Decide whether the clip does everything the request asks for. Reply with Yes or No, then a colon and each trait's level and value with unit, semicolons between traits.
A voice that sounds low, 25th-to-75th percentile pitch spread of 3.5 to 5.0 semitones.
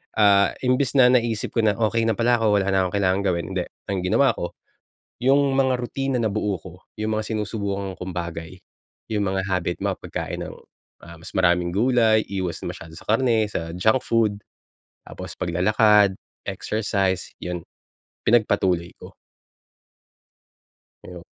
Yes: low, 105 Hz; average, 3.8 semitones